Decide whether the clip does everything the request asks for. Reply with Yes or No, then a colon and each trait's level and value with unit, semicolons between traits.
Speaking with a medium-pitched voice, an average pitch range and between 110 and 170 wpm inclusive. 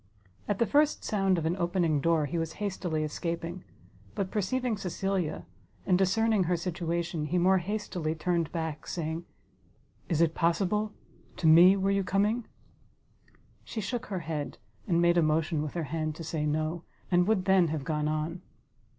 Yes: medium, 175 Hz; average, 3.2 semitones; average, 165 wpm